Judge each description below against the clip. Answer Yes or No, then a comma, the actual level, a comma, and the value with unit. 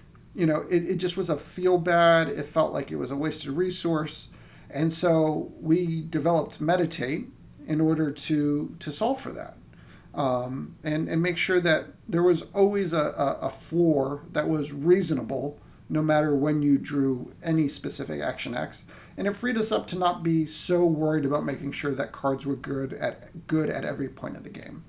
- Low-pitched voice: No, medium, 155 Hz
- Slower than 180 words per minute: No, average, 190 wpm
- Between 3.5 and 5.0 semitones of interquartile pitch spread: No, average, 2.9 semitones